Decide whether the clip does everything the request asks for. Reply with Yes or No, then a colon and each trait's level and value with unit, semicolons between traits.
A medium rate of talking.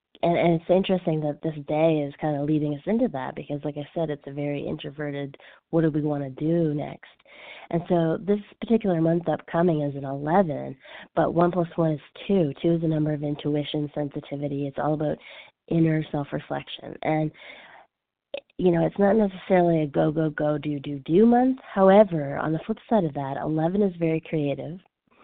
Yes: average, 195 wpm